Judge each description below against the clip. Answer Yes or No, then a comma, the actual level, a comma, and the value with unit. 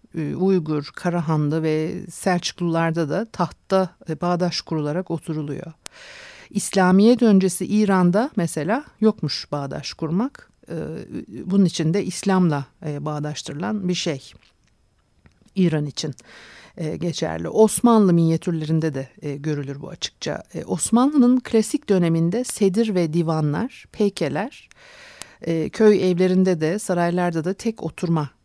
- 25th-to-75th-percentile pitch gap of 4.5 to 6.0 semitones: No, average, 4.1 semitones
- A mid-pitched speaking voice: Yes, medium, 175 Hz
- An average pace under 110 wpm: Yes, slow, 95 wpm